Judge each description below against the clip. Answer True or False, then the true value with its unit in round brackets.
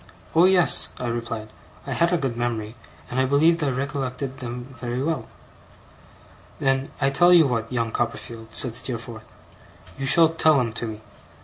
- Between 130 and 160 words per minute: False (170 wpm)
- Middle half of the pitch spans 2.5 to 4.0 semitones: True (3.4 semitones)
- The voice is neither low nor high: False (130 Hz)